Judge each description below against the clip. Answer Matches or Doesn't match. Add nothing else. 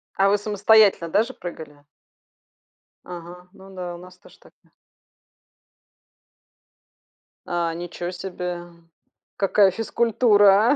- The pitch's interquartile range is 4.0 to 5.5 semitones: Doesn't match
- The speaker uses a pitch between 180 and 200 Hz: Matches